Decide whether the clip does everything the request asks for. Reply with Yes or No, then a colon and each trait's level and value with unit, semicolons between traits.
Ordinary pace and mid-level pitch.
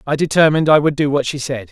No: fast, 280 wpm; medium, 145 Hz